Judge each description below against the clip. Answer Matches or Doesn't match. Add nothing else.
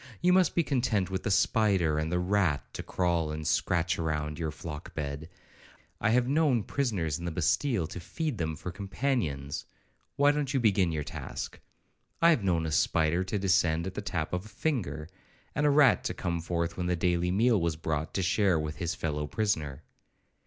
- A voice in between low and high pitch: Doesn't match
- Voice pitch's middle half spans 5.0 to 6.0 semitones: Matches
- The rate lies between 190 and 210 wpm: Matches